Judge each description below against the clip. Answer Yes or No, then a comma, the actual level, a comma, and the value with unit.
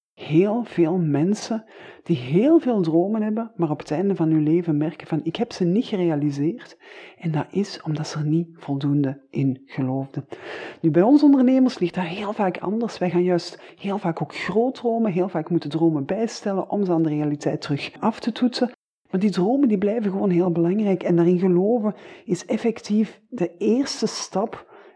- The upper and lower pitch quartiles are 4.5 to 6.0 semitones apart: Yes, average, 5.1 semitones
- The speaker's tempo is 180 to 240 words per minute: Yes, average, 190 wpm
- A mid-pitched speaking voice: Yes, medium, 180 Hz